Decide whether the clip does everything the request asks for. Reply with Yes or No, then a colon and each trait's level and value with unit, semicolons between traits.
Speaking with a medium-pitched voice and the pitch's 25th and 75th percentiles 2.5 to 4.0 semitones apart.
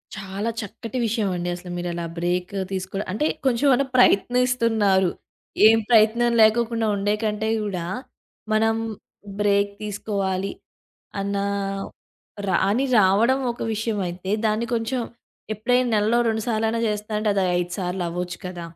No: high, 210 Hz; average, 3.1 semitones